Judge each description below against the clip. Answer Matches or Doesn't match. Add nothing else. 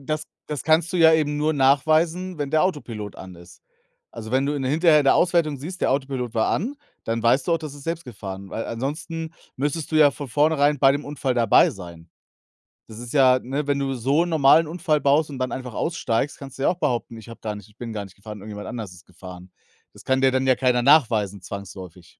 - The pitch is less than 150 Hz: Matches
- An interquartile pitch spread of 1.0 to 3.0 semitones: Doesn't match